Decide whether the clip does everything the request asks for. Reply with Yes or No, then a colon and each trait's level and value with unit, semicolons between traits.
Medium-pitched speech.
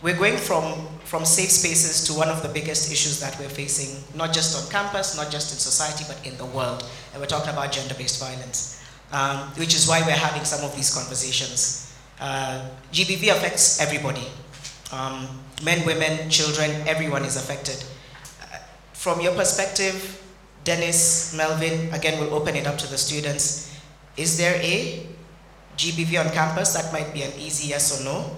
Yes: medium, 150 Hz